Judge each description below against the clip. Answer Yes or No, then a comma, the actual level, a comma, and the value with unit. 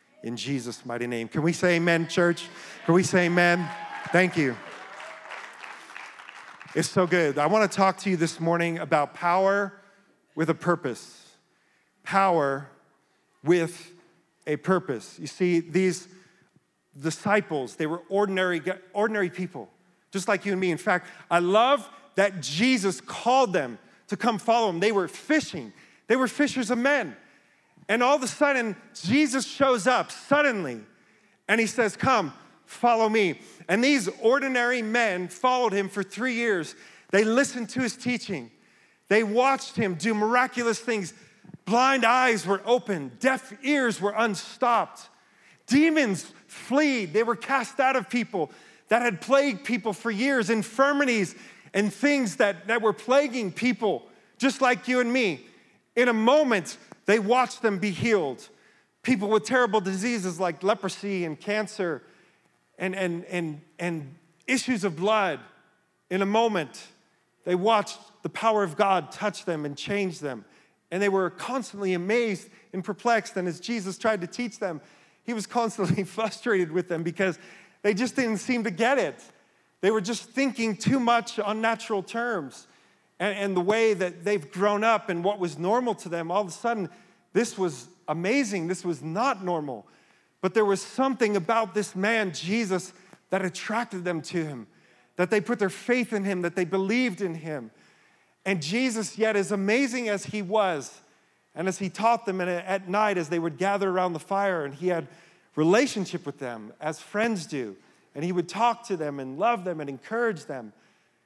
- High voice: Yes, high, 200 Hz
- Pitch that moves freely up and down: No, average, 4.7 semitones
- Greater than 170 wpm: No, average, 165 wpm